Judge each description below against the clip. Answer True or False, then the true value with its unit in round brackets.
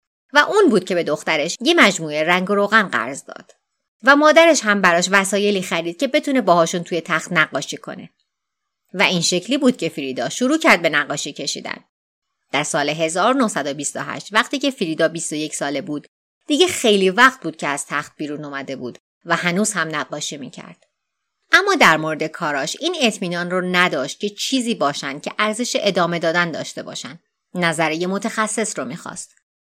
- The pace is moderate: False (165 wpm)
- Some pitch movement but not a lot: False (6.5 semitones)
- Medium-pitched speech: True (180 Hz)